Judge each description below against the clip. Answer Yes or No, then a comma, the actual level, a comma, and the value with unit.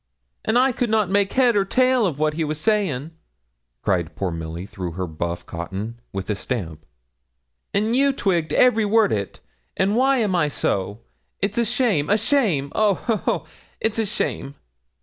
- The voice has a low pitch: No, high, 190 Hz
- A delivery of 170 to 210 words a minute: Yes, average, 180 wpm